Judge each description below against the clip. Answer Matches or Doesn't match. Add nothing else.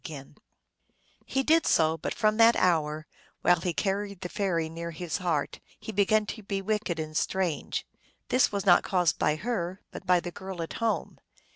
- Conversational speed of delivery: Matches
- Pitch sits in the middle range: Matches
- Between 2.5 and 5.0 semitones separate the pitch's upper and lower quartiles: Matches